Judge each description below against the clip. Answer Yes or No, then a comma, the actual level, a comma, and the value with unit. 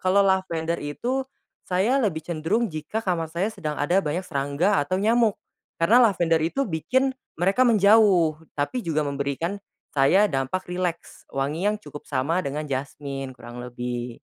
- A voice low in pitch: No, medium, 170 Hz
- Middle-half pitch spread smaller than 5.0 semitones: No, wide, 5.6 semitones